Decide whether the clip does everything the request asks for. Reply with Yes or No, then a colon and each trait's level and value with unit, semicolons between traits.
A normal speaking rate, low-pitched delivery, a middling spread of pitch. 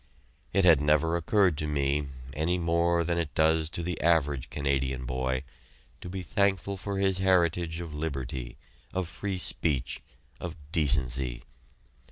Yes: average, 145 wpm; very low, 80 Hz; average, 4.1 semitones